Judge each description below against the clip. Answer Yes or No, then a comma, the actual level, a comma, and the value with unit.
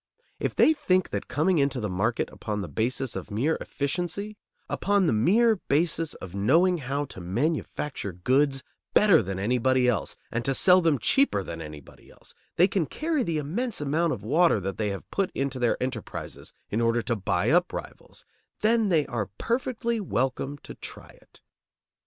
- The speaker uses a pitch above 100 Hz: Yes, medium, 140 Hz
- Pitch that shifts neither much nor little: No, wide, 8.3 semitones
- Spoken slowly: No, average, 175 wpm